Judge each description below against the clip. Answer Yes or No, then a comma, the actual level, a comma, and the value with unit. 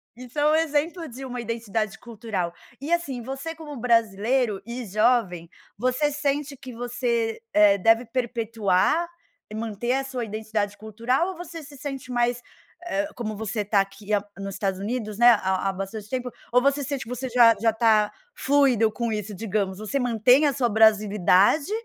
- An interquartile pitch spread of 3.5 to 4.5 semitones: Yes, average, 3.9 semitones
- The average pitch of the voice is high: Yes, high, 230 Hz